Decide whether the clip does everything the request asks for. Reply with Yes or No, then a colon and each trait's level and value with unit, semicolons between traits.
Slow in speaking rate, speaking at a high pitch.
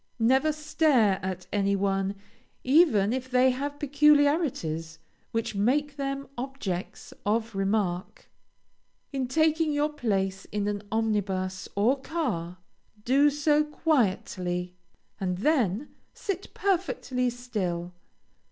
Yes: slow, 105 wpm; high, 240 Hz